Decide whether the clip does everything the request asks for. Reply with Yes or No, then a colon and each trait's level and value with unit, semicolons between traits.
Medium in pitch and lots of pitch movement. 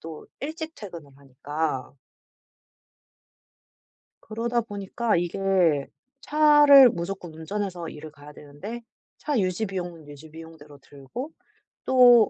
Yes: medium, 180 Hz; wide, 7.4 semitones